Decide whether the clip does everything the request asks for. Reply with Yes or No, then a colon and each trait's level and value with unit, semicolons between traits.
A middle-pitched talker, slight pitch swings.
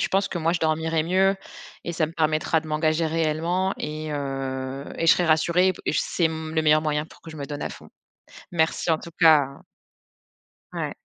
Yes: medium, 160 Hz; narrow, 1.5 semitones